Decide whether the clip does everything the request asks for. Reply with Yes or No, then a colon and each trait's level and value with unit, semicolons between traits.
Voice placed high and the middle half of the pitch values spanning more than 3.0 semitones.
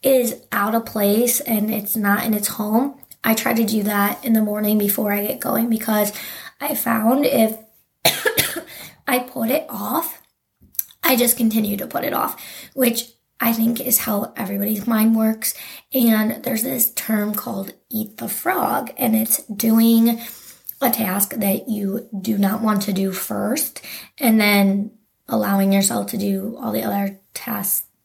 No: high, 220 Hz; narrow, 2.4 semitones